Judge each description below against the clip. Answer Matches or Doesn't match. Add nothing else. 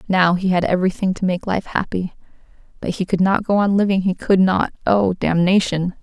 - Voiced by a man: Doesn't match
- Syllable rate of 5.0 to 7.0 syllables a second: Matches